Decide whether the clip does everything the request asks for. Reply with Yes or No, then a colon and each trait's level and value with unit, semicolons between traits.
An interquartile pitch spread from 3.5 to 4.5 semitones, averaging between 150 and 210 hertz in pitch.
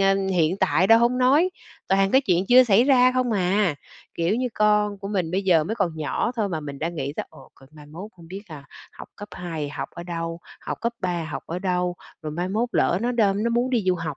No: average, 5.0 semitones; high, 190 Hz